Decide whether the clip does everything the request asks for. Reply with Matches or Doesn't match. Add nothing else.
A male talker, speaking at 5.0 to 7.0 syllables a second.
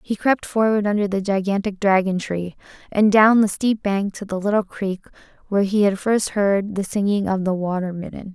Doesn't match